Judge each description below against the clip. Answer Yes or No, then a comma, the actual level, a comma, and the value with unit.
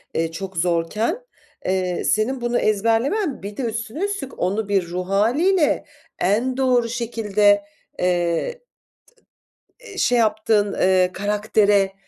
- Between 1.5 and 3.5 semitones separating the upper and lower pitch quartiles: No, average, 4.1 semitones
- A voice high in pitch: Yes, high, 210 Hz